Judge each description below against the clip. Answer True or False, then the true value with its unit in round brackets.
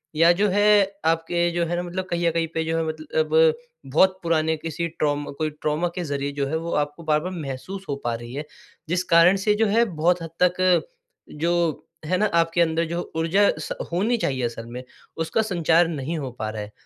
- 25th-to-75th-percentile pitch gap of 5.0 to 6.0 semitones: False (2.8 semitones)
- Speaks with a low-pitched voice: False (165 Hz)